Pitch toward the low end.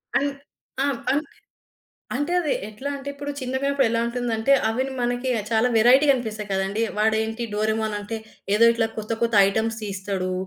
No: high, 230 Hz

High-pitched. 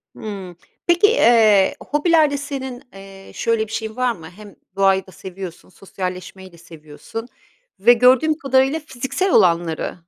Yes: high, 220 Hz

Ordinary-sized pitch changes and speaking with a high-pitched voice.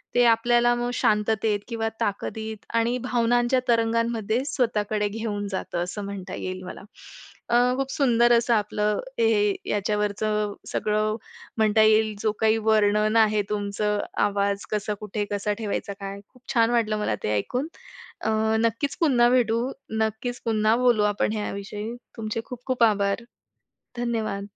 No: narrow, 2.0 semitones; high, 220 Hz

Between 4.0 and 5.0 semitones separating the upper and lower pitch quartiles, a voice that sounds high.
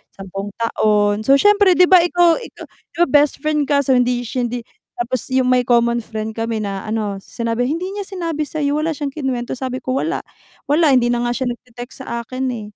Yes: average, 4.4 semitones; very high, 255 Hz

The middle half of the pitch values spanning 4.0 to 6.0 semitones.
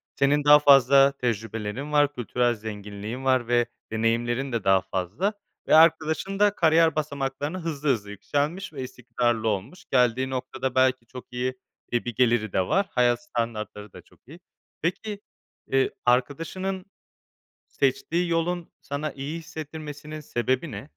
Yes: average, 4.5 semitones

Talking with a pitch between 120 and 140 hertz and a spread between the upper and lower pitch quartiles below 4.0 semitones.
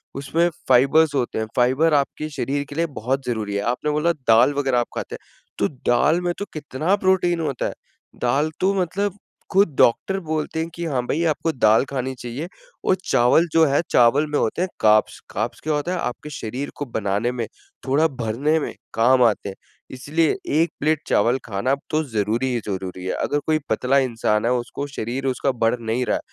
No: low, 135 Hz; average, 4.8 semitones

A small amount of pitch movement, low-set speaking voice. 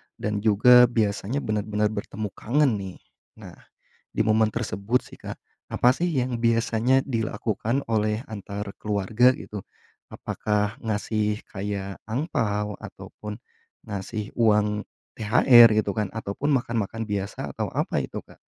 Yes: narrow, 2.3 semitones; low, 110 Hz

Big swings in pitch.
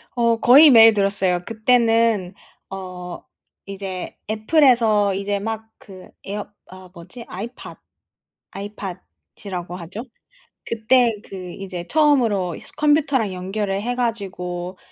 No: average, 3.7 semitones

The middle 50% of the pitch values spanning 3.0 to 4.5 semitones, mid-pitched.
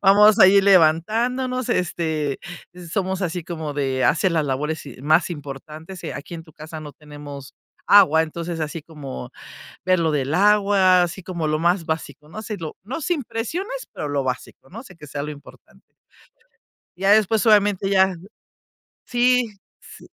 No: average, 4.9 semitones; medium, 170 Hz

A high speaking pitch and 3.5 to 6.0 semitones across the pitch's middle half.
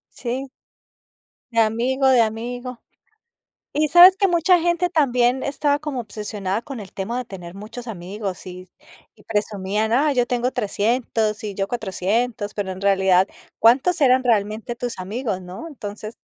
Yes: high, 230 Hz; average, 4.2 semitones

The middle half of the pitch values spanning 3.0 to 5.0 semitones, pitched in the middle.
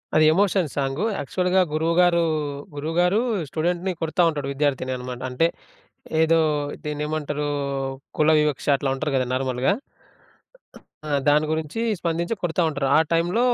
Yes: average, 3.5 semitones; medium, 155 Hz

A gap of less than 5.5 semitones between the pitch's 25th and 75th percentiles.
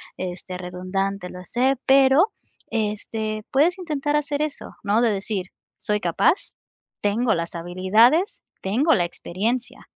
No: wide, 6.6 semitones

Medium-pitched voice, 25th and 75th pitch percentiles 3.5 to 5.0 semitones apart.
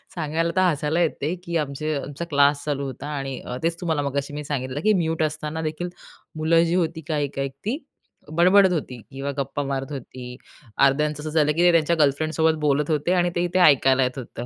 No: medium, 150 Hz; average, 3.0 semitones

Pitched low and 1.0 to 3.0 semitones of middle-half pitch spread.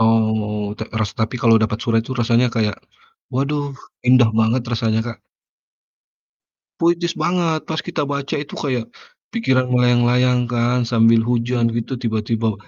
Yes: low, 120 Hz; narrow, 2.4 semitones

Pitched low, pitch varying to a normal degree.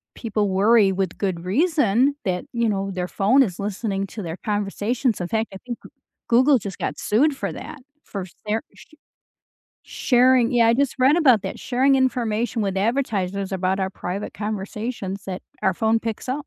No: high, 215 Hz; average, 4.2 semitones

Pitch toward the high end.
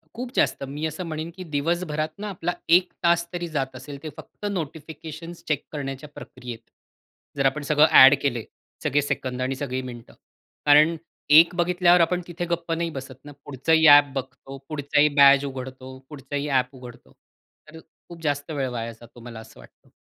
No: medium, 145 Hz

